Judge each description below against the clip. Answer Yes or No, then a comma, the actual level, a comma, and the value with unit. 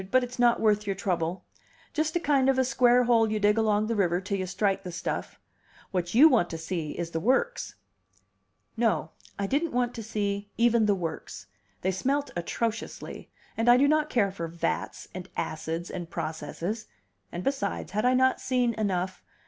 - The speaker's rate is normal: Yes, average, 190 wpm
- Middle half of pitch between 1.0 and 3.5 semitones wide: No, average, 5.2 semitones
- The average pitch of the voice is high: Yes, high, 210 Hz